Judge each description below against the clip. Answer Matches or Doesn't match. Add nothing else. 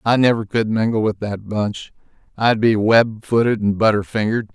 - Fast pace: Doesn't match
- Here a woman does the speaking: Doesn't match